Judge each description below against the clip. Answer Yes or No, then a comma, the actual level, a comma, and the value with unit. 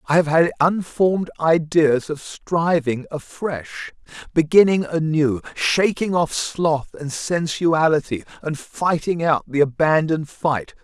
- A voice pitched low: No, medium, 160 Hz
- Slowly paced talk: Yes, slow, 115 wpm